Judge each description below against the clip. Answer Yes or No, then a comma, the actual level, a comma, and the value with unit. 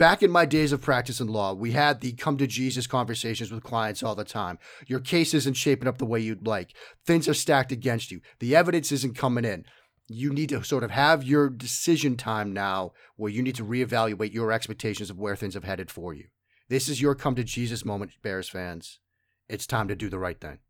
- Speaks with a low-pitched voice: Yes, low, 120 Hz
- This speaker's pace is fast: Yes, fast, 230 wpm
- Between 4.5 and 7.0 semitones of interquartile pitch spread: Yes, average, 4.8 semitones